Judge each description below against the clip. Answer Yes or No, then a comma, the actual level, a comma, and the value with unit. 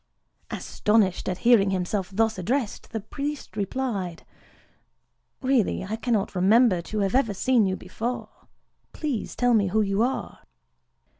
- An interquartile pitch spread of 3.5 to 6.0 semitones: Yes, average, 4.1 semitones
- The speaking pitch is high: Yes, high, 215 Hz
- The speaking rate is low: Yes, slow, 130 wpm